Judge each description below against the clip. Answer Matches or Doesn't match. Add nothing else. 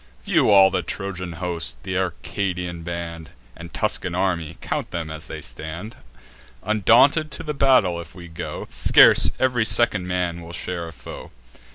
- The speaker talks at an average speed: Matches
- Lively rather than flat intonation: Doesn't match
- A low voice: Matches